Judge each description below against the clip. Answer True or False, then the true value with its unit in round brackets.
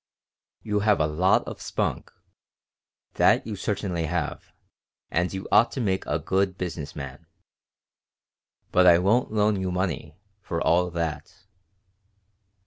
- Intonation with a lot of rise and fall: False (2.9 semitones)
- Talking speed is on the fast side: False (135 wpm)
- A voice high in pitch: False (90 Hz)